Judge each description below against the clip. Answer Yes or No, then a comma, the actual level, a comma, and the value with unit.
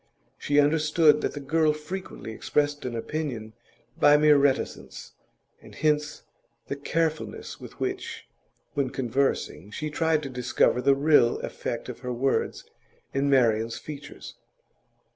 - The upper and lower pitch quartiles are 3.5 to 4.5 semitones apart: No, average, 2.9 semitones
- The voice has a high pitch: No, medium, 145 Hz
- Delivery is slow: Yes, slow, 130 wpm